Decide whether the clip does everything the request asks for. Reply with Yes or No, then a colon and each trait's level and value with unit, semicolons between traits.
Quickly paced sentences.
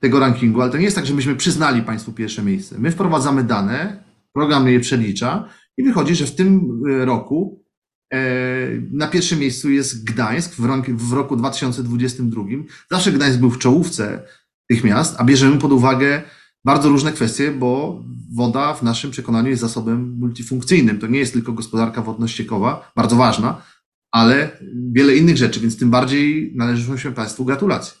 Yes: fast, 165 wpm